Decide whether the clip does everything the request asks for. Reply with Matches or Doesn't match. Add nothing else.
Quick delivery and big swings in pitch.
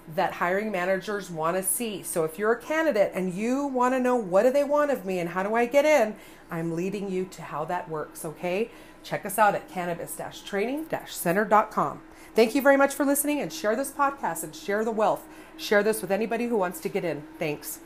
Matches